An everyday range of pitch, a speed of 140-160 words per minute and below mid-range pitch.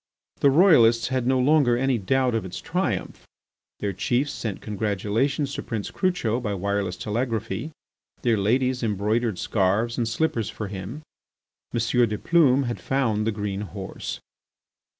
Yes: average, 4.0 semitones; average, 145 wpm; low, 115 Hz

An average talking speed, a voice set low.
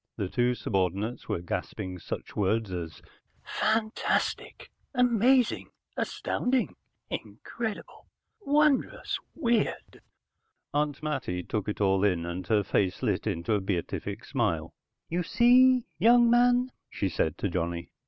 No: slow, 120 wpm; low, 115 Hz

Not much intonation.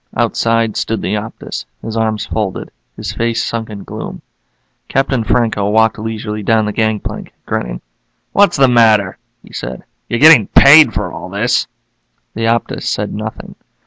Yes: narrow, 1.6 semitones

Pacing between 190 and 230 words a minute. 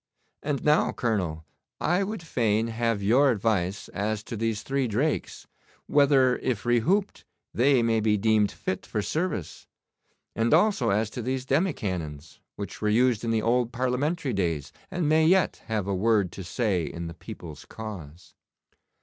No: average, 160 wpm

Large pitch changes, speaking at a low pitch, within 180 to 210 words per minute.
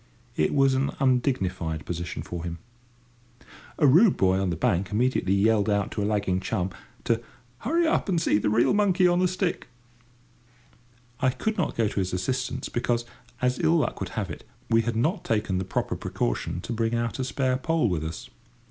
Yes: wide, 6.3 semitones; low, 115 Hz; average, 190 wpm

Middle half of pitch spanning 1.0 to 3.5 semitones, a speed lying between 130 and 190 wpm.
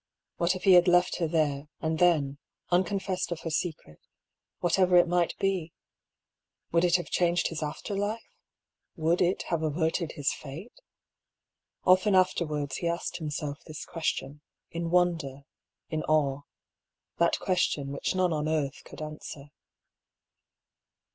Yes: average, 2.8 semitones; average, 140 wpm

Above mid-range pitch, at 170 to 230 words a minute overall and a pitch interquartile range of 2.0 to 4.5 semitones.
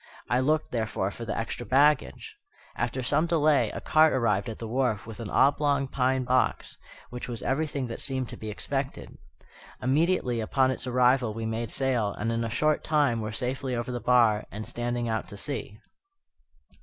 No: low, 125 Hz; average, 180 wpm; average, 3.0 semitones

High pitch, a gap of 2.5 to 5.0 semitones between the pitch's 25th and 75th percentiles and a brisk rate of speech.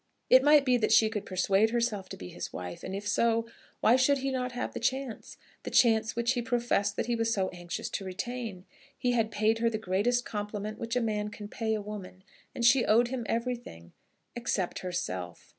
Yes: high, 225 Hz; average, 3.3 semitones; fast, 210 wpm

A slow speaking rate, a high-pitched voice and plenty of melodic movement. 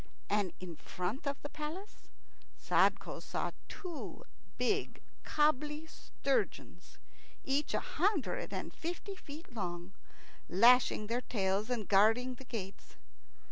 Yes: slow, 115 wpm; very high, 250 Hz; wide, 6.9 semitones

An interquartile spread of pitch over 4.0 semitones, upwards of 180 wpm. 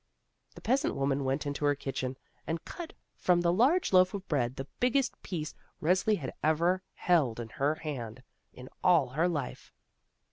No: average, 5.3 semitones; average, 170 wpm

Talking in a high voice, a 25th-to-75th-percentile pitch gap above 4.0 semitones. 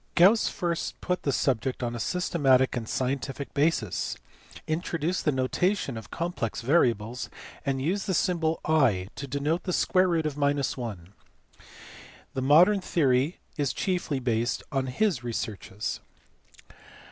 No: medium, 140 Hz; average, 5.3 semitones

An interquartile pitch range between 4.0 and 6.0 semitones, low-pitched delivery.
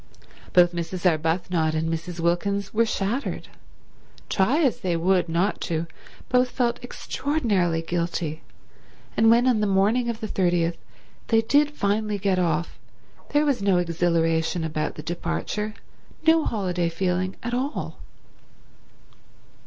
No: average, 5.0 semitones; medium, 185 Hz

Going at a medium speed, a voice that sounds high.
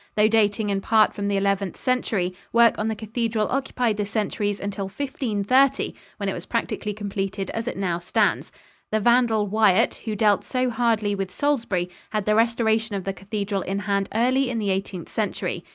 Yes: average, 185 wpm; high, 210 Hz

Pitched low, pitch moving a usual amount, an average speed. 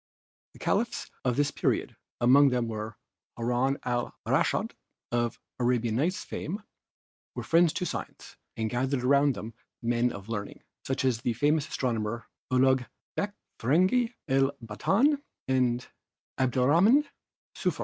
No: low, 130 Hz; average, 3.6 semitones; slow, 130 wpm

